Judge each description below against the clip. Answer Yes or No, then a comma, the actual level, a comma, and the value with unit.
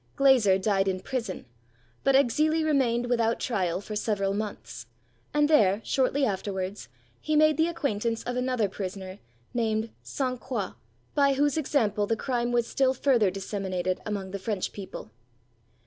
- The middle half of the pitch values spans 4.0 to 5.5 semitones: Yes, average, 5.2 semitones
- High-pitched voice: Yes, high, 225 Hz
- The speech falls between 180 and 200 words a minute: No, average, 145 wpm